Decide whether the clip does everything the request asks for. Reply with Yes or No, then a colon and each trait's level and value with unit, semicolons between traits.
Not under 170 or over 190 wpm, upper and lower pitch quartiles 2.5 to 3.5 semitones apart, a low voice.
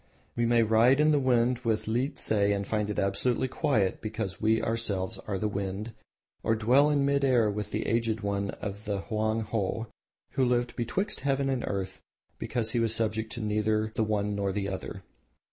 Yes: average, 185 wpm; average, 2.8 semitones; low, 110 Hz